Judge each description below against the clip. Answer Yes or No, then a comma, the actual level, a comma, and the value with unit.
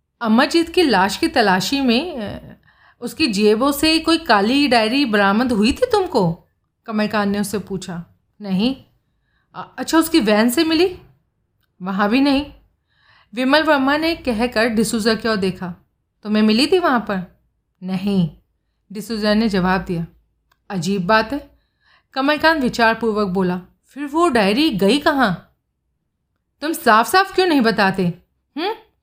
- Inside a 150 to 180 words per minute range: No, average, 135 wpm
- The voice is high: Yes, high, 225 Hz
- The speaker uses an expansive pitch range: Yes, wide, 6.9 semitones